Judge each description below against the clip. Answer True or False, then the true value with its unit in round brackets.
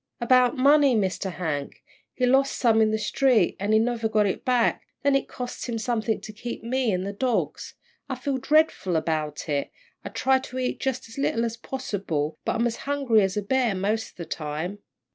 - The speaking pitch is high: True (230 Hz)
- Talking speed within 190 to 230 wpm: True (200 wpm)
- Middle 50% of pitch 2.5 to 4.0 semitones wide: False (4.7 semitones)